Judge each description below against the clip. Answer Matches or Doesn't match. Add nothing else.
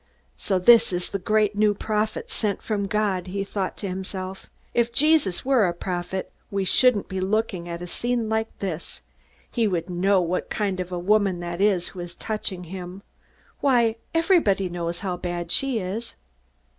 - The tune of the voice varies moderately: Matches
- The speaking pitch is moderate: Doesn't match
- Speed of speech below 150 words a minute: Doesn't match